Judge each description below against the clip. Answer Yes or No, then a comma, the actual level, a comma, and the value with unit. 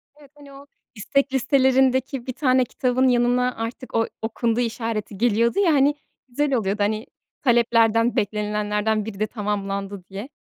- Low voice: No, high, 235 Hz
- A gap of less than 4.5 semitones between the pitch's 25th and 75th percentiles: Yes, average, 3.7 semitones